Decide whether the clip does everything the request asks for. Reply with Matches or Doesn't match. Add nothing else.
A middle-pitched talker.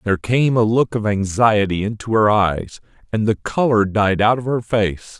Doesn't match